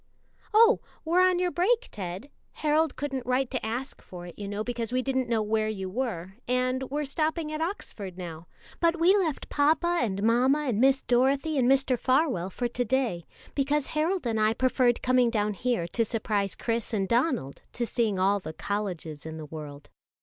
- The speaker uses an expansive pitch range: Yes, wide, 5.9 semitones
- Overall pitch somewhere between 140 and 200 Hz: No, high, 245 Hz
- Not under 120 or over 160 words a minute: No, average, 190 wpm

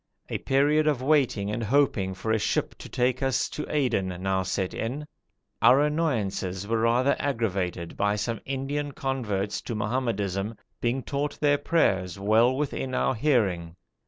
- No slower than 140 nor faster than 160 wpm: Yes, average, 155 wpm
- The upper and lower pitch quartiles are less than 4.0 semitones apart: No, wide, 5.5 semitones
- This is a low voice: Yes, low, 120 Hz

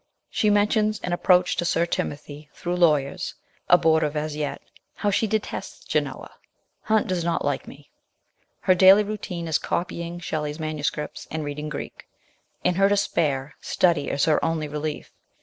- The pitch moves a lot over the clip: No, average, 3.6 semitones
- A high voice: No, medium, 170 Hz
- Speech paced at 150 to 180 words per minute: Yes, average, 165 wpm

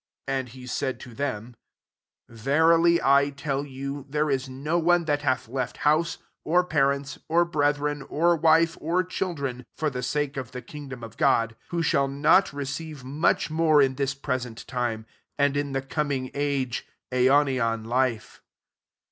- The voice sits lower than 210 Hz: Yes, medium, 140 Hz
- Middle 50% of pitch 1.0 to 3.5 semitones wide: Yes, average, 2.8 semitones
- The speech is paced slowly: No, average, 165 wpm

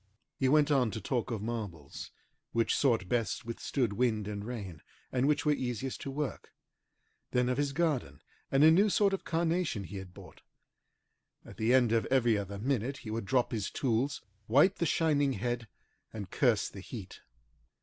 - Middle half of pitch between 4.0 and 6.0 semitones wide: Yes, average, 4.6 semitones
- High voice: No, low, 120 Hz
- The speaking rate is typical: Yes, average, 180 wpm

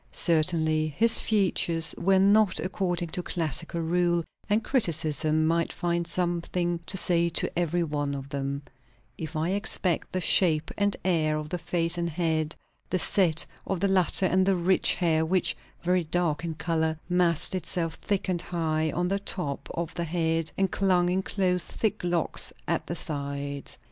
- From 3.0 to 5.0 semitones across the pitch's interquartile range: No, narrow, 2.4 semitones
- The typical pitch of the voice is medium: Yes, medium, 170 Hz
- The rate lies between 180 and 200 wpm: No, average, 170 wpm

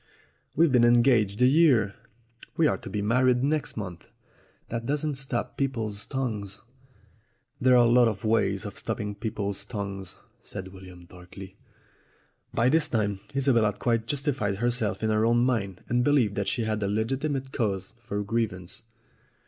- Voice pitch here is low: Yes, low, 115 Hz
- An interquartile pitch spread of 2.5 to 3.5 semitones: No, average, 3.9 semitones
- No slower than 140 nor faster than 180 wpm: Yes, average, 155 wpm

